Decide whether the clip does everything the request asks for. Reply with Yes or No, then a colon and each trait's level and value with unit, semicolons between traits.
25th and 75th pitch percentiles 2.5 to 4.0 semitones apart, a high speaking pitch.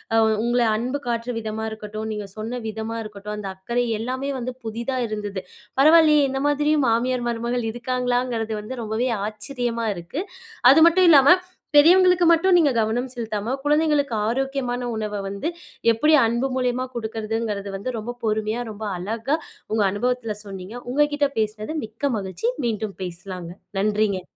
Yes: average, 3.6 semitones; high, 235 Hz